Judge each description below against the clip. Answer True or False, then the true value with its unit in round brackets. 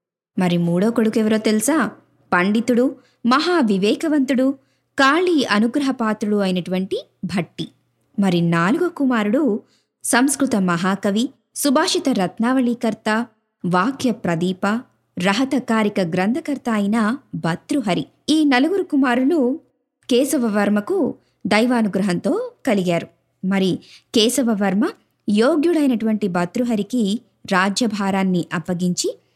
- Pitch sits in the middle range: False (225 Hz)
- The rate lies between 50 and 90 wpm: True (80 wpm)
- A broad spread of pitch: True (5.7 semitones)